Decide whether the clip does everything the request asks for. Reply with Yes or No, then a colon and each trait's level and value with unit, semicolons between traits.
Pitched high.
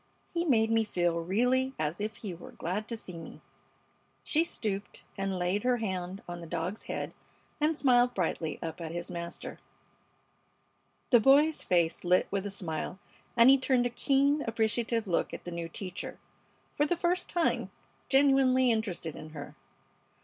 Yes: high, 215 Hz